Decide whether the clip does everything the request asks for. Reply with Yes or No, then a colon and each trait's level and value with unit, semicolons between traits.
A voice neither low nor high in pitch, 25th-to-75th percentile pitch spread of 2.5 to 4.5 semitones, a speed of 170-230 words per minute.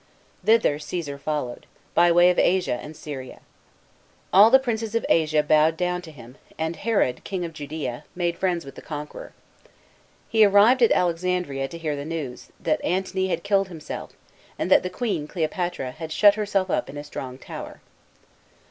Yes: medium, 170 Hz; average, 4.1 semitones; average, 175 wpm